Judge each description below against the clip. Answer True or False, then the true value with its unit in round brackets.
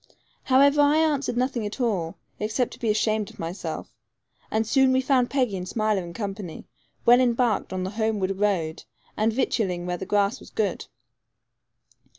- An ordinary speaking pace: True (165 wpm)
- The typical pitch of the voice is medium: False (215 Hz)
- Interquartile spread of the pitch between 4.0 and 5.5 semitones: True (4.6 semitones)